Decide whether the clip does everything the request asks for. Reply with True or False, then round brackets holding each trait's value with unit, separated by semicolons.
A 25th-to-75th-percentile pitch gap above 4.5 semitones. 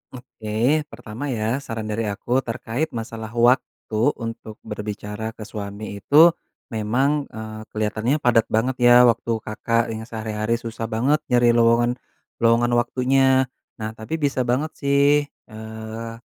False (2.7 semitones)